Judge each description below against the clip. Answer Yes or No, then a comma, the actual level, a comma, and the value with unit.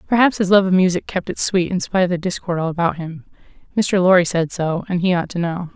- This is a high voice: No, medium, 180 Hz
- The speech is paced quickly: Yes, fast, 260 wpm